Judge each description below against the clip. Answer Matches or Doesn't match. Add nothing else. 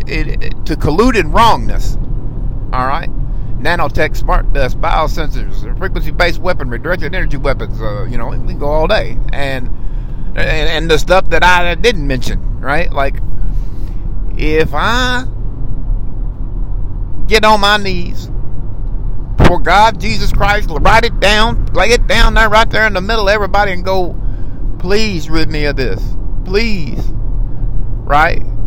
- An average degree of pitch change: Doesn't match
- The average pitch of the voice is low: Matches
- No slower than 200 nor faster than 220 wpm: Doesn't match